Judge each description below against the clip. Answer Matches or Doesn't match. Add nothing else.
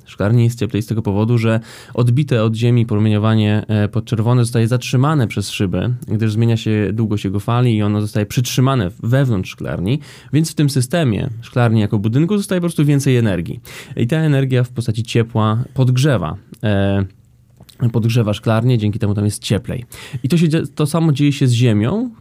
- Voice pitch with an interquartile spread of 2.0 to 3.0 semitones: Doesn't match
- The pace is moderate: Doesn't match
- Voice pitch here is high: Doesn't match